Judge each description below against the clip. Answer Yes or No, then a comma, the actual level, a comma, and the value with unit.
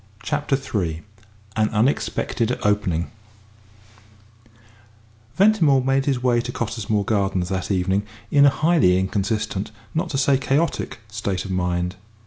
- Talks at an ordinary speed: No, slow, 120 wpm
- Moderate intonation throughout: No, wide, 6.0 semitones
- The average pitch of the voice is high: No, low, 110 Hz